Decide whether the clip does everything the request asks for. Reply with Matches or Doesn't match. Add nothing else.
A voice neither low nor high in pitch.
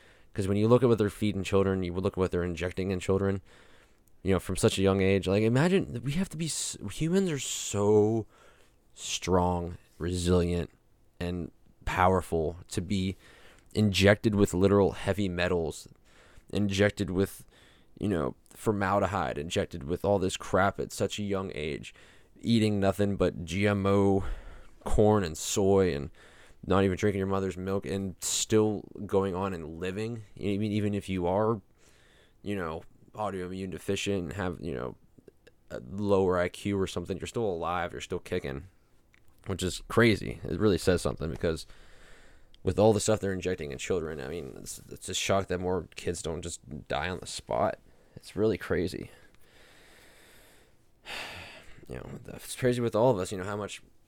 Doesn't match